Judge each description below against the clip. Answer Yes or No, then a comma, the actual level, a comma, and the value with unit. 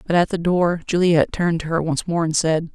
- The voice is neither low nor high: Yes, medium, 170 Hz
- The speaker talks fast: Yes, fast, 260 wpm